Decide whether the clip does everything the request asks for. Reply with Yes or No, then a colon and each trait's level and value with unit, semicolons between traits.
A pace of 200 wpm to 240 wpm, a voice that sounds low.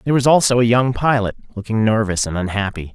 Yes: fast, 205 wpm; low, 115 Hz